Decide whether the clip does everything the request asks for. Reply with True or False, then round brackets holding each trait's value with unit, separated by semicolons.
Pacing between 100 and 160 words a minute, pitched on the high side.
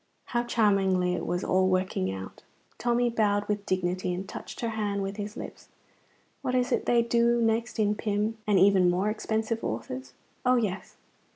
False (175 wpm; 205 Hz)